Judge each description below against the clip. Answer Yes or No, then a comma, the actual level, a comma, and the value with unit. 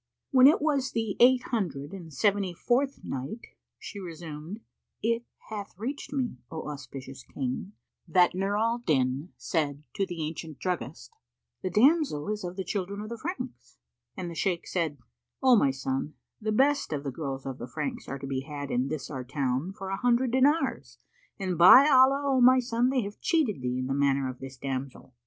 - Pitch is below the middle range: No, medium, 185 Hz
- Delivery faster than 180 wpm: Yes, average, 190 wpm